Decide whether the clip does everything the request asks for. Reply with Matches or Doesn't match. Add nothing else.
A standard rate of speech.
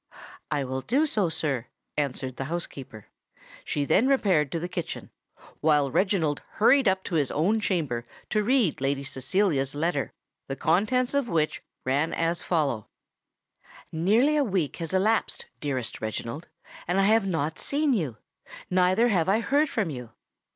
Matches